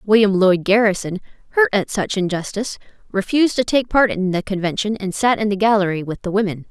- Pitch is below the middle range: No, high, 205 Hz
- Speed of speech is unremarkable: Yes, average, 195 wpm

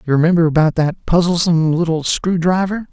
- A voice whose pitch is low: No, medium, 170 Hz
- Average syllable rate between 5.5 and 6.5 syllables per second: Yes, 6.0 syllables/s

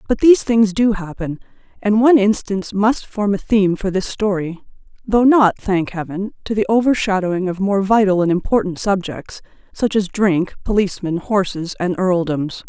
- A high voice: Yes, high, 200 Hz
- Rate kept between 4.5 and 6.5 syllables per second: Yes, 5.1 syllables/s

